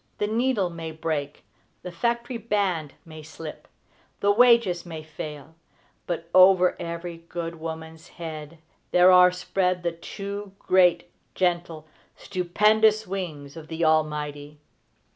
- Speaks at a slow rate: Yes, slow, 125 wpm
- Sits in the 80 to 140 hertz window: No, medium, 175 Hz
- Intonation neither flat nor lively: Yes, average, 3.3 semitones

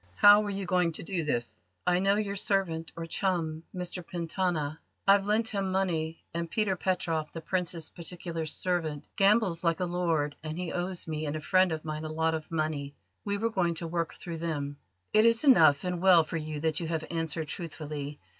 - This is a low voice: No, medium, 170 Hz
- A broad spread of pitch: No, average, 3.0 semitones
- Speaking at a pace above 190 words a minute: Yes, average, 200 wpm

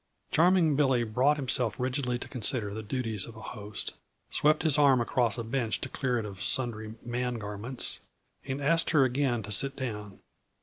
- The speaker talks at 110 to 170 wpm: No, average, 180 wpm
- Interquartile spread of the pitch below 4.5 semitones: Yes, average, 3.8 semitones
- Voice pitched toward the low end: Yes, low, 125 Hz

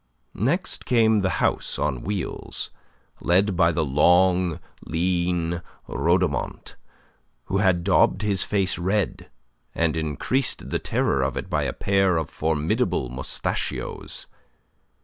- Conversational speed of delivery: No, slow, 120 wpm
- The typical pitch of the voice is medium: No, very low, 90 Hz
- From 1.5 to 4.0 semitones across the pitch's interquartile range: Yes, average, 3.2 semitones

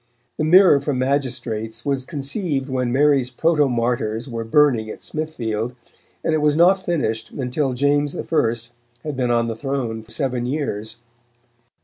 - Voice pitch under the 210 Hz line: Yes, low, 135 Hz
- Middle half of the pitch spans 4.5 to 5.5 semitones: No, average, 3.8 semitones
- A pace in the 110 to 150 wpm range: Yes, average, 140 wpm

